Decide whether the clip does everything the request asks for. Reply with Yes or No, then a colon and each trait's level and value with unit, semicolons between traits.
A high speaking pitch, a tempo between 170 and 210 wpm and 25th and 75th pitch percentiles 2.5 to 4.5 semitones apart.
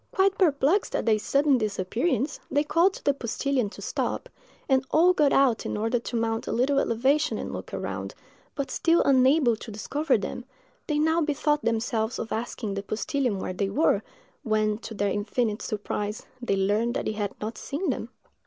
No: high, 245 Hz; average, 185 wpm; average, 5.2 semitones